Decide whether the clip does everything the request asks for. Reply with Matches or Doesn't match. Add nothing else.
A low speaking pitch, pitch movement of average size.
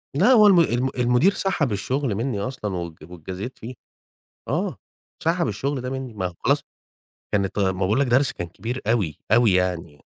Doesn't match